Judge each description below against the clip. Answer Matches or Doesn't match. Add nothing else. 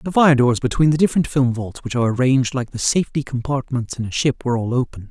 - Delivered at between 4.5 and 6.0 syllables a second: Doesn't match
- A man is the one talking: Doesn't match